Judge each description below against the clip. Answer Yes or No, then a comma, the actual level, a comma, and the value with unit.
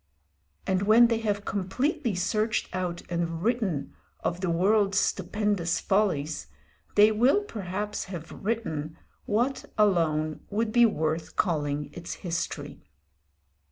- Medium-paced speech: No, slow, 120 wpm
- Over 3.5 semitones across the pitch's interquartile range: Yes, average, 4.2 semitones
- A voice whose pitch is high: Yes, high, 195 Hz